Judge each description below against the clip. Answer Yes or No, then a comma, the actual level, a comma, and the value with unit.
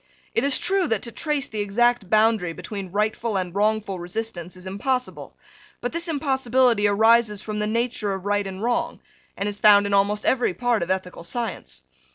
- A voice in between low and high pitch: No, high, 210 Hz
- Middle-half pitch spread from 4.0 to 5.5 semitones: No, average, 3.4 semitones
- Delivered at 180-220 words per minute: Yes, average, 185 wpm